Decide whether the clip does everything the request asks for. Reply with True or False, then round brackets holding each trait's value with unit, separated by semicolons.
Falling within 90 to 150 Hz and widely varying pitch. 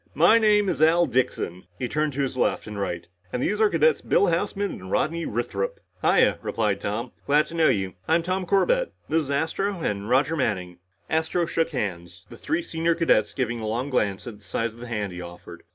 True (135 Hz; 8.3 semitones)